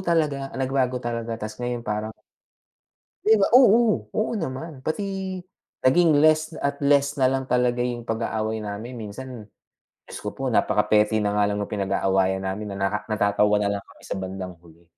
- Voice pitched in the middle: No, low, 120 Hz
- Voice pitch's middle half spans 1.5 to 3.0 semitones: No, average, 4.9 semitones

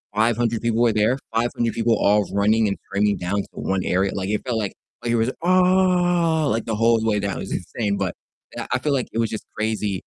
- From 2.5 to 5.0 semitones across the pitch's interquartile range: Yes, average, 2.8 semitones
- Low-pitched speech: Yes, low, 110 Hz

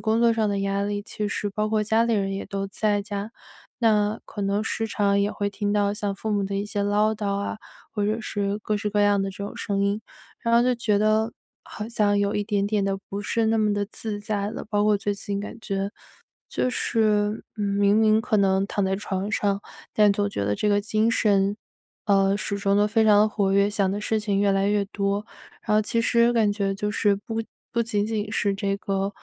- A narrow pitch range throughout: Yes, narrow, 1.3 semitones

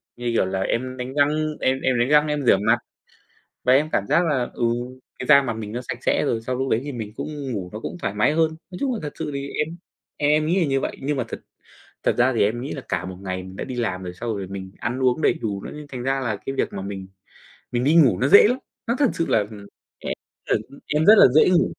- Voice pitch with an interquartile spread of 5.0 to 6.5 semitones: Yes, wide, 5.5 semitones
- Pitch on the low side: Yes, low, 130 Hz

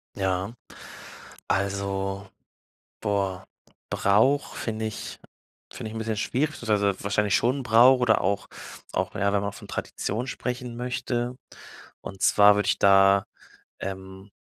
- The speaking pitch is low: Yes, low, 105 Hz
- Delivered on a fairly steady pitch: No, average, 3.3 semitones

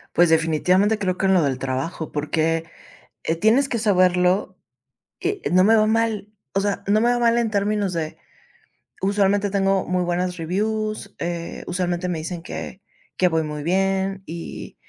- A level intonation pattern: No, average, 3.3 semitones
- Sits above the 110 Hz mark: Yes, medium, 185 Hz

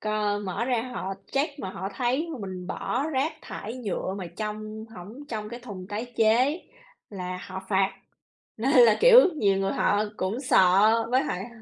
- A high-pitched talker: Yes, high, 220 Hz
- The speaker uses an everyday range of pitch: Yes, average, 4.6 semitones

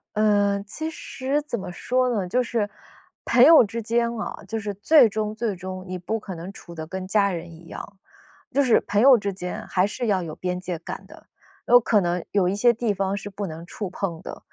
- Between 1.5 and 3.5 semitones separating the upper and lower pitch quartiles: No, average, 4.1 semitones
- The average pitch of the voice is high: Yes, high, 205 Hz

